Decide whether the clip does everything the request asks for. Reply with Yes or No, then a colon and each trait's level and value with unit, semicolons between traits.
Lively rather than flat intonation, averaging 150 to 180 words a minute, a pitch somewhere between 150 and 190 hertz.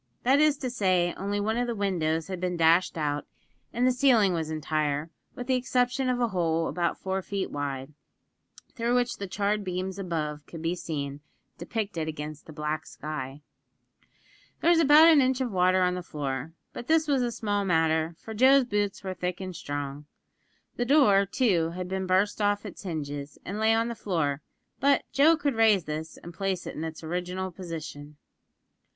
No: wide, 6.2 semitones; average, 190 wpm; medium, 185 Hz